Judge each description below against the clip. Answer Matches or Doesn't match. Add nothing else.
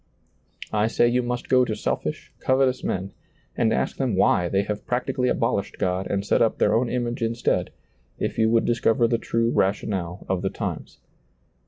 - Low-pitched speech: Matches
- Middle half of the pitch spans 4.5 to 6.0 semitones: Doesn't match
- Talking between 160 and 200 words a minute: Matches